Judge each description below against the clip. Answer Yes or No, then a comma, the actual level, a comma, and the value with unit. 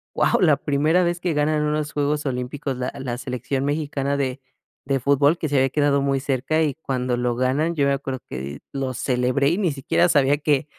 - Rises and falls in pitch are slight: Yes, narrow, 2.3 semitones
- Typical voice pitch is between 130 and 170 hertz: Yes, medium, 140 Hz